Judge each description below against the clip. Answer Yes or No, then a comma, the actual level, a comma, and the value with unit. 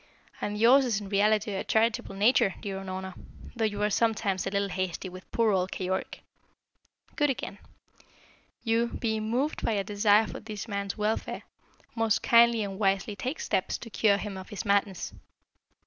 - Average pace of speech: Yes, average, 170 wpm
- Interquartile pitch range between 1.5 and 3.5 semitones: Yes, narrow, 2.5 semitones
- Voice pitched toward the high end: Yes, high, 210 Hz